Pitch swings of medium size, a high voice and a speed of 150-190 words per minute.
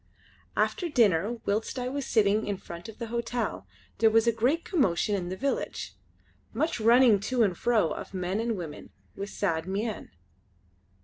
Yes: average, 3.7 semitones; high, 220 Hz; average, 170 wpm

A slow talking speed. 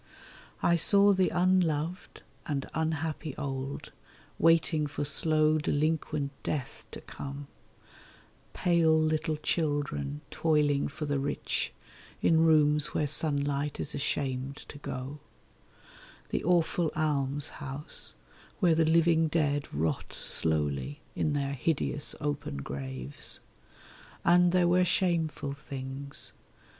Yes: slow, 105 wpm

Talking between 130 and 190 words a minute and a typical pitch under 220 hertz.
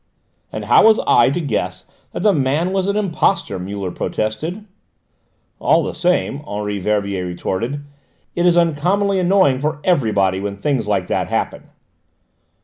Yes: average, 145 wpm; medium, 140 Hz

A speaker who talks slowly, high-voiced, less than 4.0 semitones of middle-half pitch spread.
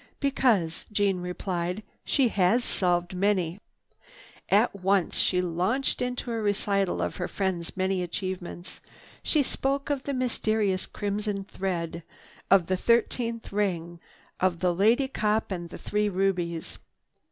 Yes: slow, 130 wpm; high, 195 Hz; average, 3.4 semitones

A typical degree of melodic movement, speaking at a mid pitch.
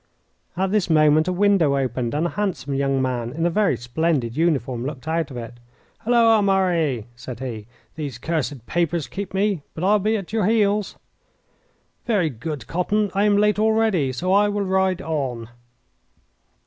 No: wide, 7.0 semitones; medium, 165 Hz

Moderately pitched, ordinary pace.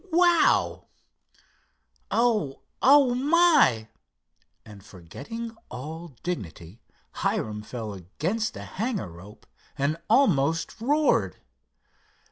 No: medium, 165 Hz; slow, 85 wpm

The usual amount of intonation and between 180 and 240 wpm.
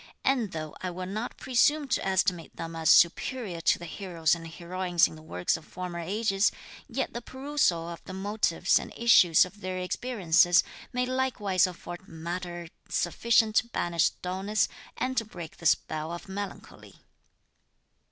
No: average, 4.5 semitones; average, 160 wpm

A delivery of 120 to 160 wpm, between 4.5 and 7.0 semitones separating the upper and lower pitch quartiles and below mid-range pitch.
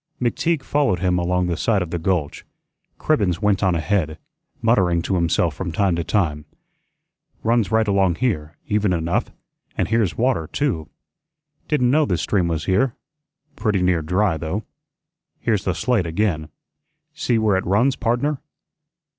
Yes: average, 155 wpm; average, 4.9 semitones; very low, 95 Hz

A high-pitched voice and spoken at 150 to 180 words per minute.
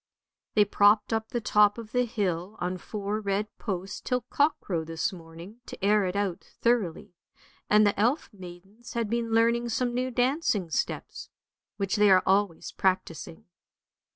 Yes: high, 205 Hz; average, 160 wpm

